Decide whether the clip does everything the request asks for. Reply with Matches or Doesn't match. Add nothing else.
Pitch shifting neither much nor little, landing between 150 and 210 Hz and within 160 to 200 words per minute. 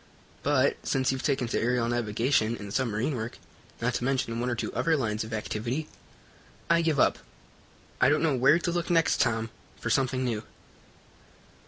Doesn't match